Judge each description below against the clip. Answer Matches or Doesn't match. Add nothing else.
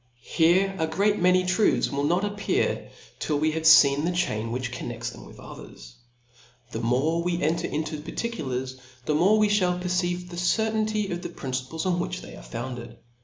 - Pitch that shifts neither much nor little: Doesn't match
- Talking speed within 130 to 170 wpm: Doesn't match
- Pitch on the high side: Doesn't match